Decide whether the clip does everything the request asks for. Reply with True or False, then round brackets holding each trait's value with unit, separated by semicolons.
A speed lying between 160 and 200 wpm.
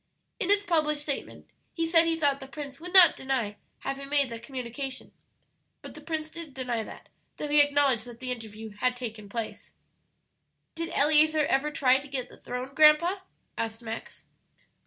True (175 wpm)